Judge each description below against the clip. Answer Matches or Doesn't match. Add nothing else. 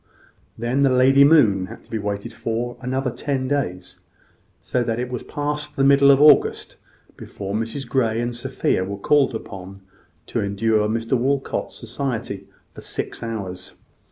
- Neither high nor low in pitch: Doesn't match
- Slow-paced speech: Doesn't match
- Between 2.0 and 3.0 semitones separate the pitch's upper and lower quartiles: Doesn't match